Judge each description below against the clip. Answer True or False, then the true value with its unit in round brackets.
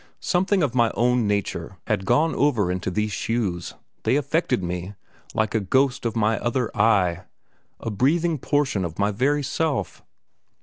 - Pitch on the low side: True (115 Hz)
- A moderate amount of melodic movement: False (5.8 semitones)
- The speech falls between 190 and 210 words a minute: False (160 wpm)